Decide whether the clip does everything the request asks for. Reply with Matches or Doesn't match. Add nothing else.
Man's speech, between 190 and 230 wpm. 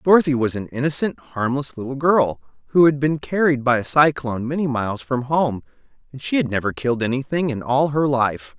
Matches